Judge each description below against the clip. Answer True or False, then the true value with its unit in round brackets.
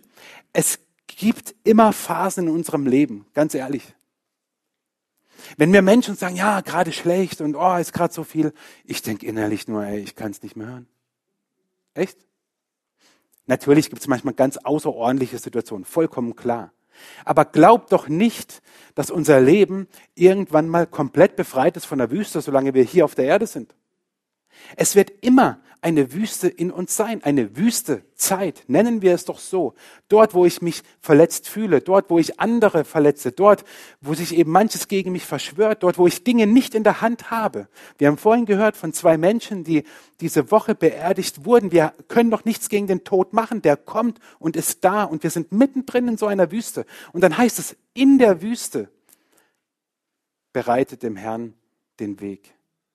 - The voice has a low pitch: False (180 Hz)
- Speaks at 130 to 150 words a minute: False (175 wpm)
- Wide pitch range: True (6.0 semitones)